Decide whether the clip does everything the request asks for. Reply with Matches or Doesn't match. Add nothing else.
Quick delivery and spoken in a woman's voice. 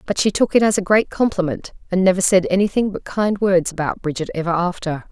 Matches